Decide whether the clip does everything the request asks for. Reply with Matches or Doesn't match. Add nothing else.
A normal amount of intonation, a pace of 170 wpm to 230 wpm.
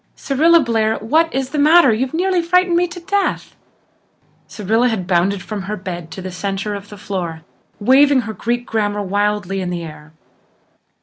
Doesn't match